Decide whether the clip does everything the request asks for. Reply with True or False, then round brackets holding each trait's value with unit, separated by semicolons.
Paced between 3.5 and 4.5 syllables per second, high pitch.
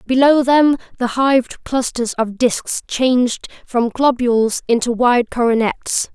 True (4.1 syllables/s; 245 Hz)